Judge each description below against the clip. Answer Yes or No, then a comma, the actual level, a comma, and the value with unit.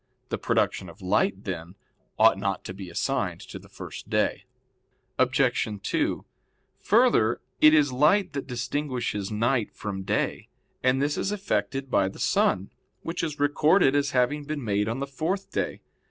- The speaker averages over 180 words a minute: No, average, 160 wpm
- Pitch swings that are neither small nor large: No, wide, 6.6 semitones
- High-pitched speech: No, low, 130 Hz